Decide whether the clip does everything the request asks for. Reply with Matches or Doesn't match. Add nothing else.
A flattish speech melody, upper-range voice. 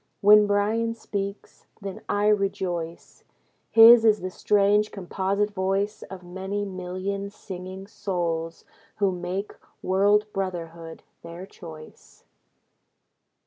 Matches